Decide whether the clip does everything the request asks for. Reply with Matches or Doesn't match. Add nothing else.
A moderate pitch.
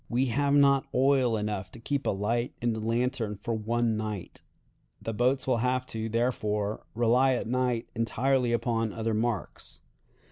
Doesn't match